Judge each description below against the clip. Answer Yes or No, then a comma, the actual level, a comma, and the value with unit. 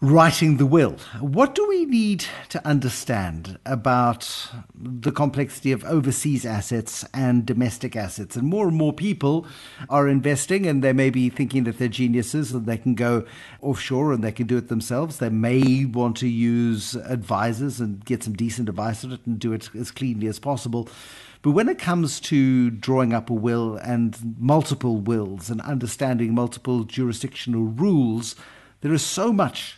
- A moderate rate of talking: Yes, average, 170 wpm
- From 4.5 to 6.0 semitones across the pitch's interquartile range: No, average, 3.3 semitones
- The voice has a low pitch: Yes, low, 125 Hz